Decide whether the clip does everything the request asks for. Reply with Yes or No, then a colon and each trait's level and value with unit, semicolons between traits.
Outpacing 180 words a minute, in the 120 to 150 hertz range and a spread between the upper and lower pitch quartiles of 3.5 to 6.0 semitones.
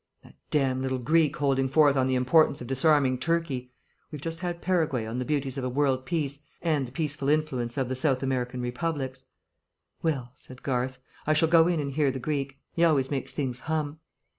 No: average, 200 wpm; medium, 140 Hz; average, 3.1 semitones